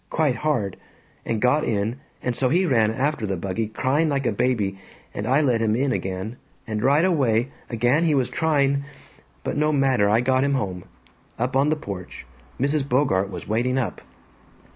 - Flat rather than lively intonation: No, average, 4.6 semitones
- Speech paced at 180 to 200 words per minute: Yes, average, 185 wpm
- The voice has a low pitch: Yes, low, 125 Hz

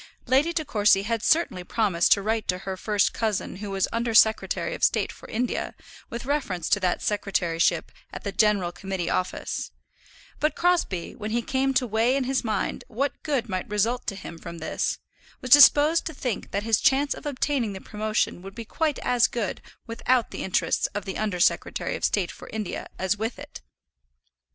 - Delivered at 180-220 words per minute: Yes, average, 190 wpm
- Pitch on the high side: Yes, high, 220 Hz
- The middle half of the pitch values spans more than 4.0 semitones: Yes, average, 4.7 semitones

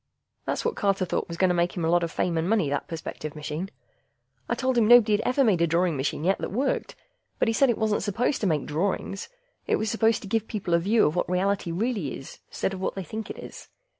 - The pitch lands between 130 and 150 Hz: No, high, 190 Hz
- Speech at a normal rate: No, fast, 255 wpm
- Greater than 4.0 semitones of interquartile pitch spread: Yes, average, 4.7 semitones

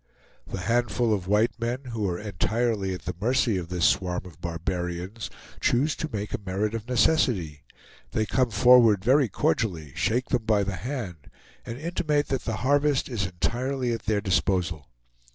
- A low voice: Yes, low, 110 Hz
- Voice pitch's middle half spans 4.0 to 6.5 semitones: Yes, average, 5.1 semitones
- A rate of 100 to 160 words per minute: No, average, 170 wpm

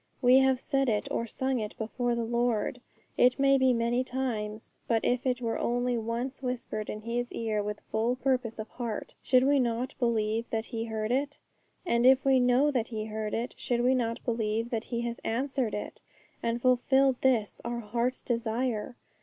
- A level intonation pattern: Yes, narrow, 2.1 semitones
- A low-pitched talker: No, high, 240 Hz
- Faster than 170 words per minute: Yes, average, 190 wpm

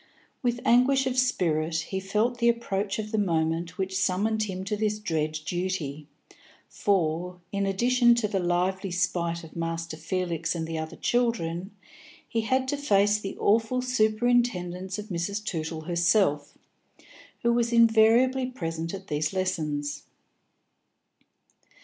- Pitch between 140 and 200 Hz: Yes, high, 190 Hz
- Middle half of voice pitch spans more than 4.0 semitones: Yes, average, 5.1 semitones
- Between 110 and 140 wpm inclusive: Yes, slow, 135 wpm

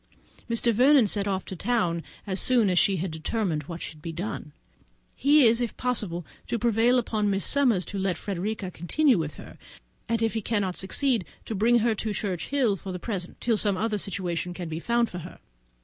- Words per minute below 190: No, average, 200 wpm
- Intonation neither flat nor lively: Yes, average, 4.4 semitones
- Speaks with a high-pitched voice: Yes, high, 205 Hz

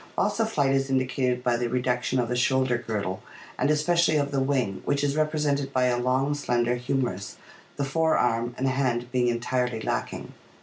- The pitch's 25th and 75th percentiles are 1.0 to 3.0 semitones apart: Yes, narrow, 2.4 semitones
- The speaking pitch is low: Yes, low, 130 Hz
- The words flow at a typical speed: Yes, average, 185 wpm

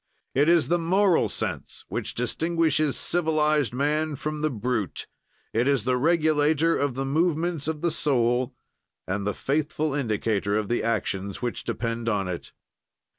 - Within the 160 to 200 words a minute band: No, average, 150 wpm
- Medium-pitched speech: Yes, medium, 145 Hz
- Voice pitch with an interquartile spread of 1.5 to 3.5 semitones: No, average, 5.1 semitones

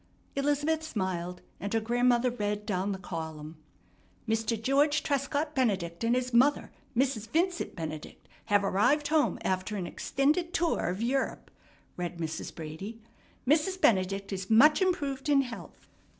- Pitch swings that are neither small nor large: No, wide, 7.1 semitones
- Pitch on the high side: Yes, high, 230 Hz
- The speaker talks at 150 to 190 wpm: No, average, 140 wpm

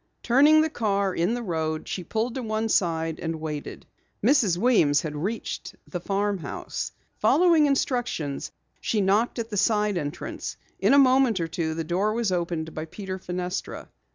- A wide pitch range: Yes, wide, 6.1 semitones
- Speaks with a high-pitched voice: Yes, high, 195 Hz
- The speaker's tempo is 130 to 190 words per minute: Yes, average, 165 wpm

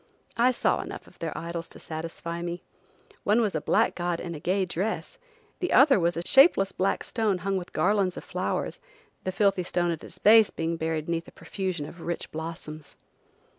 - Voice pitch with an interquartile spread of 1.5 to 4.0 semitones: Yes, average, 3.1 semitones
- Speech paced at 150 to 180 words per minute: No, average, 195 wpm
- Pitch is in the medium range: Yes, medium, 175 Hz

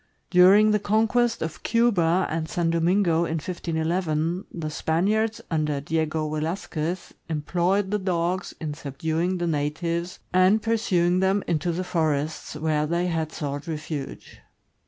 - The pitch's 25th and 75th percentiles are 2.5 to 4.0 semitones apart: Yes, average, 2.9 semitones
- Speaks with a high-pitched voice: No, medium, 170 Hz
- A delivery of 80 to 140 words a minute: Yes, slow, 135 wpm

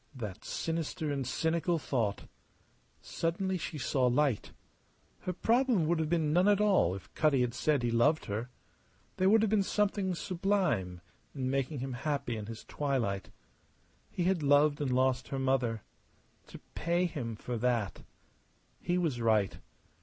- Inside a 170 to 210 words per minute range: No, average, 155 wpm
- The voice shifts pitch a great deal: Yes, wide, 6.2 semitones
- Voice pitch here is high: No, medium, 145 Hz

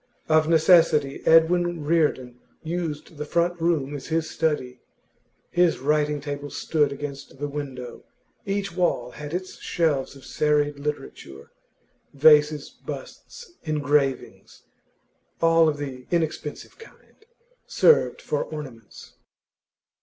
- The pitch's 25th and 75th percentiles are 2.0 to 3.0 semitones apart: Yes, narrow, 2.6 semitones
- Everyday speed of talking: No, slow, 110 wpm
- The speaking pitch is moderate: Yes, medium, 150 Hz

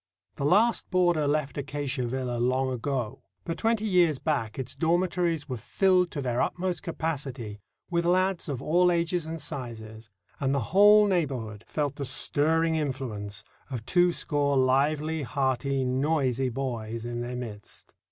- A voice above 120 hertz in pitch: Yes, medium, 140 Hz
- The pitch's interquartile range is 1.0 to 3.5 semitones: No, average, 4.9 semitones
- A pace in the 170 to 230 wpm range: No, average, 145 wpm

